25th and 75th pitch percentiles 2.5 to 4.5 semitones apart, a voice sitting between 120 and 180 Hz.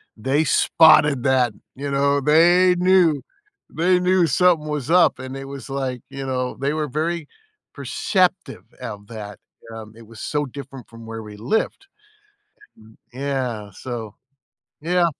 No: average, 5.2 semitones; medium, 140 Hz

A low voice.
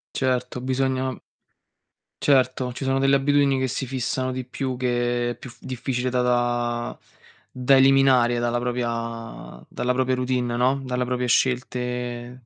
Yes: low, 125 Hz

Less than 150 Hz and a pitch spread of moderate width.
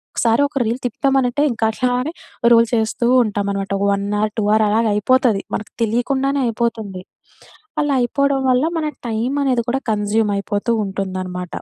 No: high, 230 Hz; average, 3.7 semitones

